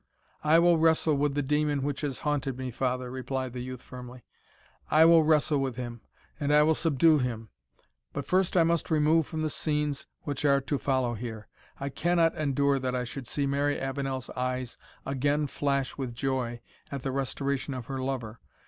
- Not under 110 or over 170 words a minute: No, average, 185 wpm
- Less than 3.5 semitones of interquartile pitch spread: Yes, average, 2.7 semitones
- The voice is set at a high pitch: No, medium, 140 Hz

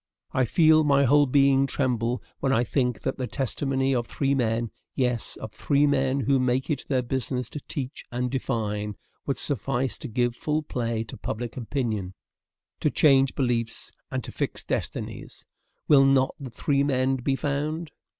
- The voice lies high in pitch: No, low, 130 Hz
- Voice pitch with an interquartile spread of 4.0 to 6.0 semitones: No, narrow, 2.5 semitones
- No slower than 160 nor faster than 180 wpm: Yes, average, 170 wpm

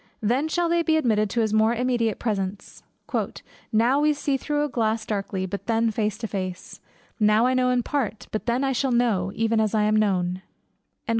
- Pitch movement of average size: Yes, average, 3.1 semitones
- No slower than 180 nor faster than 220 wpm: Yes, average, 200 wpm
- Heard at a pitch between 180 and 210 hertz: No, high, 225 Hz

